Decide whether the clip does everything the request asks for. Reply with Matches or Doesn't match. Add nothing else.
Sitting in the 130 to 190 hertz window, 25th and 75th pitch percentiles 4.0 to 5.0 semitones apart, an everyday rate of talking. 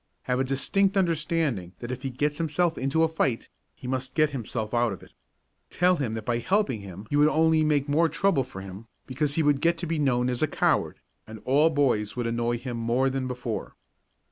Doesn't match